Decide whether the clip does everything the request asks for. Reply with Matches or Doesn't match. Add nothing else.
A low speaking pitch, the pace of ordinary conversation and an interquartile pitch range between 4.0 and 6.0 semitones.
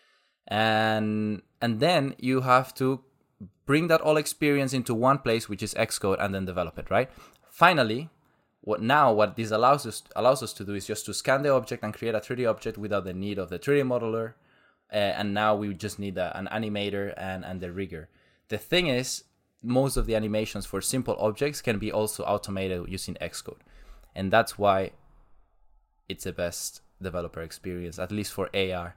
Matches